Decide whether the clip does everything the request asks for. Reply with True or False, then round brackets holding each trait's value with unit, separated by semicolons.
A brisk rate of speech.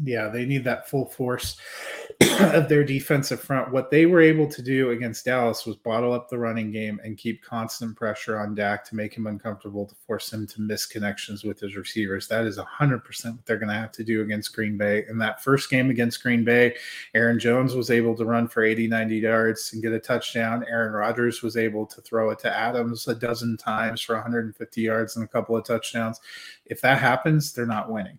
True (220 wpm)